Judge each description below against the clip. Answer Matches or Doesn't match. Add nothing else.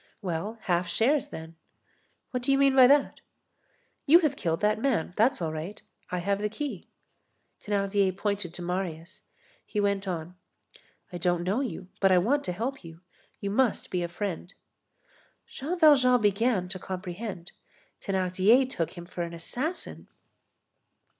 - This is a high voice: Matches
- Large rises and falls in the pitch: Matches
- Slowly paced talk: Doesn't match